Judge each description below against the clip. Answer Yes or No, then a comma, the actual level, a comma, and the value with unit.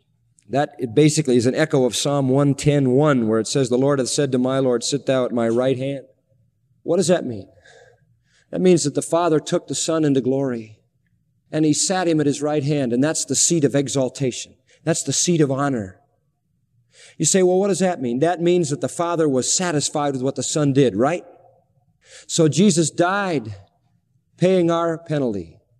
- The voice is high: No, medium, 140 Hz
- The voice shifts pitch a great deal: No, average, 3.6 semitones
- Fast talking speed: No, average, 195 wpm